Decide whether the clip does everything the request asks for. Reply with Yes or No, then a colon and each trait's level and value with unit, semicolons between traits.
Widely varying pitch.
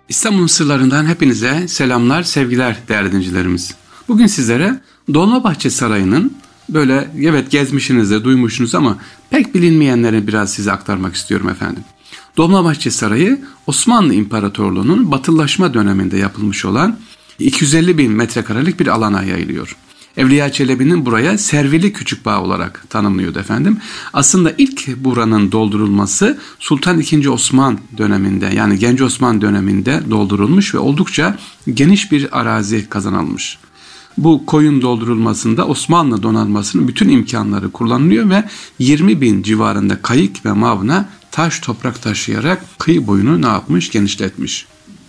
Yes: wide, 7.3 semitones